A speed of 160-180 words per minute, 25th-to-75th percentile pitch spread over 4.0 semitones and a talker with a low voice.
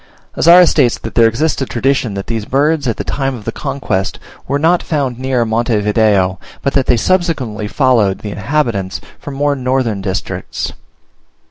Yes: average, 170 wpm; average, 4.6 semitones; low, 125 Hz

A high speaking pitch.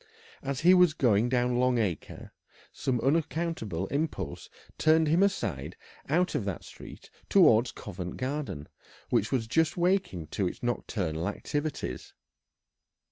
No: low, 130 Hz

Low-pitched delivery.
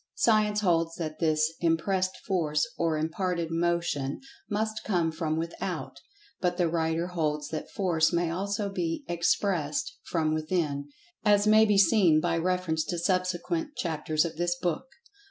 No: medium, 170 Hz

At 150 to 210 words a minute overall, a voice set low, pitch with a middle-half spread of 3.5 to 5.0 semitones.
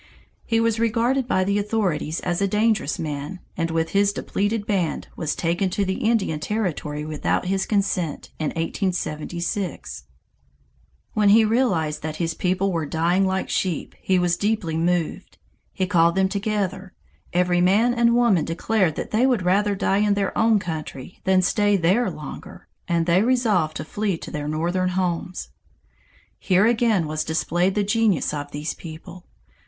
No: average, 160 wpm; medium, 185 Hz; average, 4.0 semitones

